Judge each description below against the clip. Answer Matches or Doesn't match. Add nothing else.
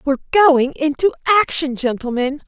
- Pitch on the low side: Doesn't match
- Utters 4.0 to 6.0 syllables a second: Matches